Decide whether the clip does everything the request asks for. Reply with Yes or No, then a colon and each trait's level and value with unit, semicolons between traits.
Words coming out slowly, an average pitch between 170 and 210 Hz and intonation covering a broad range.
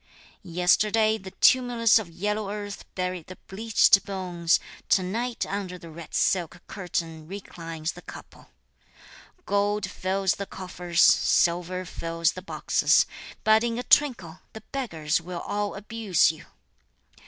No: slow, 130 wpm; high, 190 Hz; average, 3.5 semitones